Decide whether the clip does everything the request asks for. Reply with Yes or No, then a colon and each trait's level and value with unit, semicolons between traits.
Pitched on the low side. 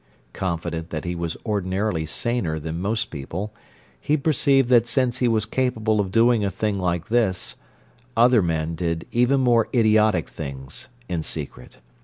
Yes: low, 105 Hz